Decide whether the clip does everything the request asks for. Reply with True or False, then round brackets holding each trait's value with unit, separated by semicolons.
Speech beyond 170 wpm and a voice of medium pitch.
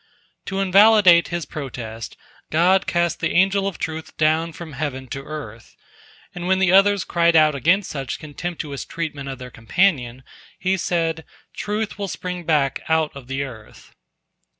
False (155 wpm; 165 Hz)